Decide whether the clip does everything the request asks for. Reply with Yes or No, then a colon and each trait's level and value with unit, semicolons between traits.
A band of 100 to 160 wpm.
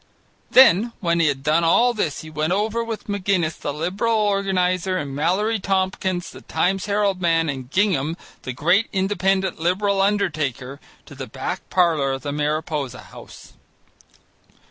Yes: average, 150 wpm